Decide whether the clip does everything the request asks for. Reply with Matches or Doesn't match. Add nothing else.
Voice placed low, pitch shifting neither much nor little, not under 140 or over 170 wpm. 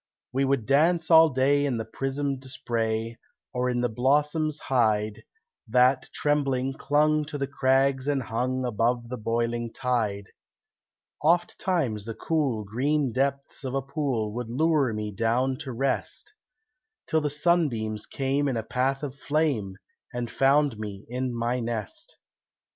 Matches